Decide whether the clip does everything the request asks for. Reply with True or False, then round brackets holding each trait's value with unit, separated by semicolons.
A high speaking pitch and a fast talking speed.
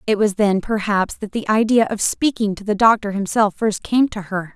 True (210 Hz; 225 wpm)